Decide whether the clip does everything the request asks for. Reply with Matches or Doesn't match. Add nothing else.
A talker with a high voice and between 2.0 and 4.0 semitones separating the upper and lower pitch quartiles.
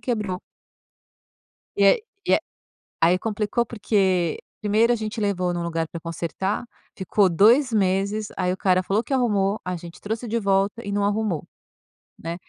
Matches